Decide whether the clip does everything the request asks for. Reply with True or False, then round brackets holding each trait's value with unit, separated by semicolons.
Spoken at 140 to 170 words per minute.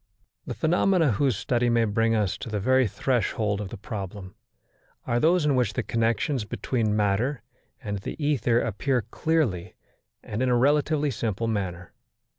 True (160 wpm)